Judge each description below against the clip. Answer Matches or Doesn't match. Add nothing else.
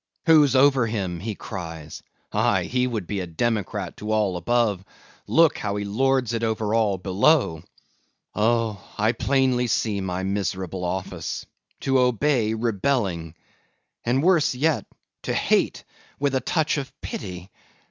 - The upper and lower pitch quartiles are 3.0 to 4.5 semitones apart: Doesn't match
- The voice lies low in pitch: Matches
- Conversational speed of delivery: Doesn't match